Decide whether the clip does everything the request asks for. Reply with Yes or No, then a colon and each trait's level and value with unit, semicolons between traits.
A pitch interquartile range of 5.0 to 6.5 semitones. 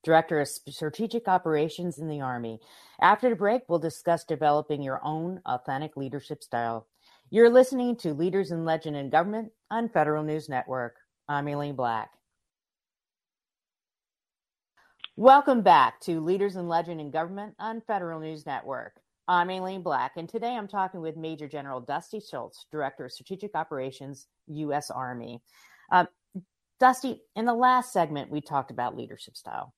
Yes: average, 5.3 semitones